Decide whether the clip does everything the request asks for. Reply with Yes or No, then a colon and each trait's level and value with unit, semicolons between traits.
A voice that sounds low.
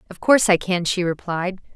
No: medium, 185 Hz